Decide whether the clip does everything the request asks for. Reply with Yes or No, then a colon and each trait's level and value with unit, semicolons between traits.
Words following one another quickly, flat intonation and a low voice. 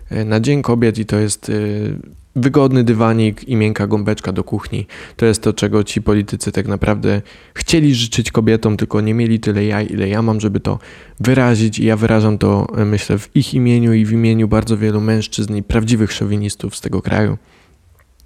Yes: fast, 180 wpm; narrow, 1.7 semitones; low, 110 Hz